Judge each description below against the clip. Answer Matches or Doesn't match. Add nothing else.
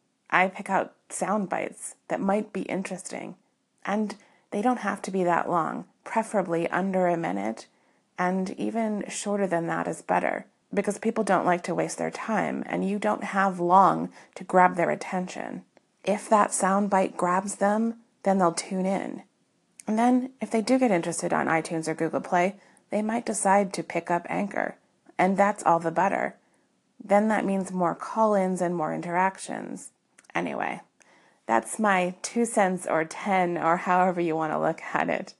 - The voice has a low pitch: Doesn't match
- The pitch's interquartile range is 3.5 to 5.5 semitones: Doesn't match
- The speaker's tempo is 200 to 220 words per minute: Doesn't match